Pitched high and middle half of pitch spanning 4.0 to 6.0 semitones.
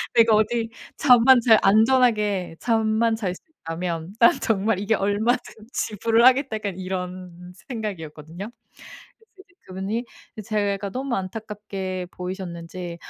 No: high, 205 Hz; average, 3.6 semitones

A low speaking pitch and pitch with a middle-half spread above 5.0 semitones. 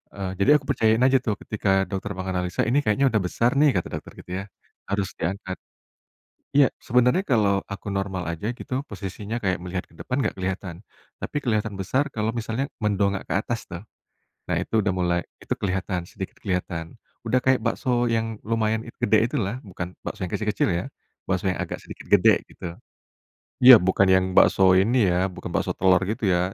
No: low, 100 Hz; average, 3.4 semitones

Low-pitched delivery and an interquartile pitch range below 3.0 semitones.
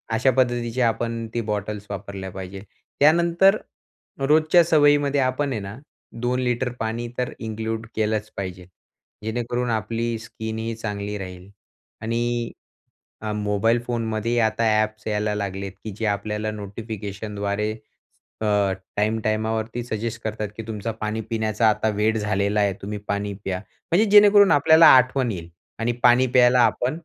Yes: low, 110 Hz; narrow, 2.6 semitones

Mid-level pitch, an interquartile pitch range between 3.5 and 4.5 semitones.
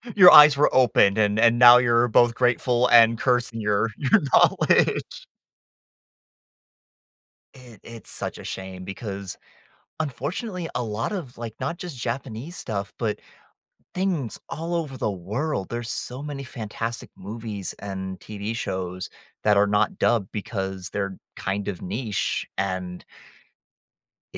No: low, 115 Hz; average, 4.1 semitones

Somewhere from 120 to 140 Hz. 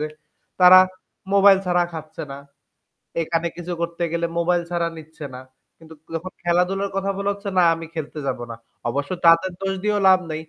No: medium, 170 Hz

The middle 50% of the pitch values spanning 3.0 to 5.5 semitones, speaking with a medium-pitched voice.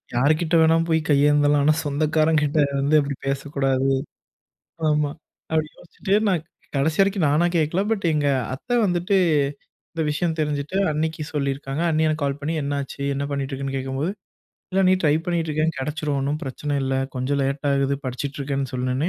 No: narrow, 2.4 semitones; medium, 145 Hz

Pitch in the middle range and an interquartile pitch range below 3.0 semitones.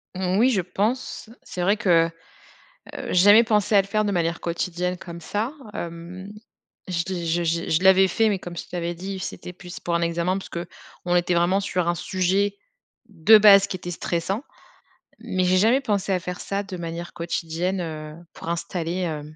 Yes: medium, 180 Hz; narrow, 2.5 semitones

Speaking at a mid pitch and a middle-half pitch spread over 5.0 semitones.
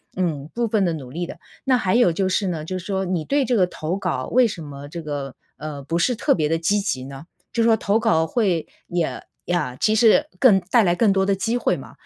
Yes: medium, 180 Hz; wide, 5.4 semitones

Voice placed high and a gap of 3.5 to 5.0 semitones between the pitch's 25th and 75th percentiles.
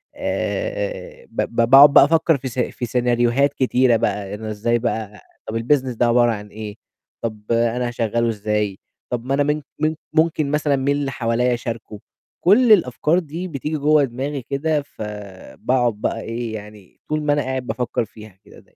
No: low, 125 Hz; average, 4.4 semitones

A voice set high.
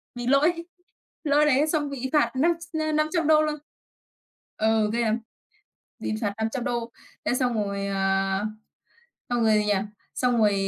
Yes: high, 245 Hz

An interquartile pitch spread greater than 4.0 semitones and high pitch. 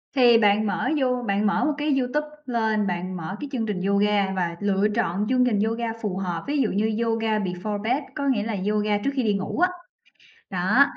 No: average, 3.7 semitones; high, 215 Hz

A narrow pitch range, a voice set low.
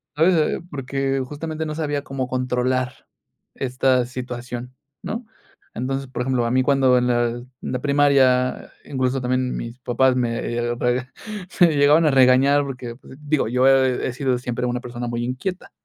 Yes: narrow, 1.9 semitones; low, 130 Hz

